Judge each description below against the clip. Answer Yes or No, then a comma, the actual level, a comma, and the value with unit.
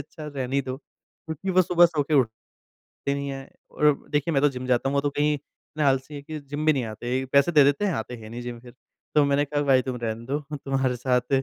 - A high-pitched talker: No, medium, 140 Hz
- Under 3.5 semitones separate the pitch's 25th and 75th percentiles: Yes, narrow, 2.6 semitones